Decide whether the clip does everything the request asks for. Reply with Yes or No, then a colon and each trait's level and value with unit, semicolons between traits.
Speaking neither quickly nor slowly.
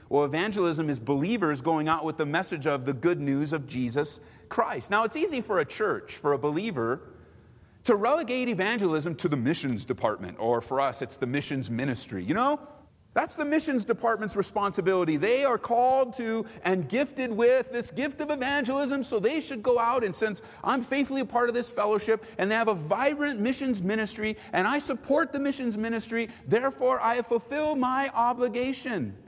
Yes: average, 180 wpm